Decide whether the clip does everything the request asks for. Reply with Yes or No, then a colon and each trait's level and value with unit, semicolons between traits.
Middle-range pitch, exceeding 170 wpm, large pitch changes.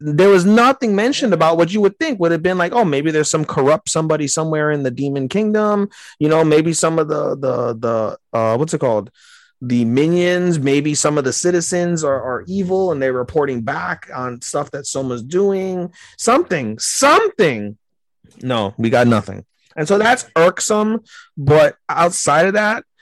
Yes: medium, 160 Hz; average, 180 wpm; wide, 6.1 semitones